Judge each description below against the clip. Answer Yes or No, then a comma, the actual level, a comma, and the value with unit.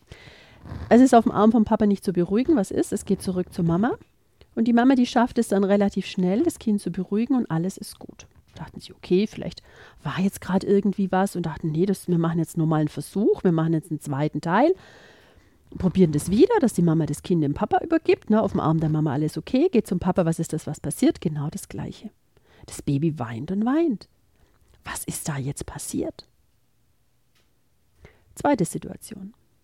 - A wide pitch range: Yes, wide, 5.7 semitones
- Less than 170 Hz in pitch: No, medium, 185 Hz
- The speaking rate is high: Yes, fast, 205 wpm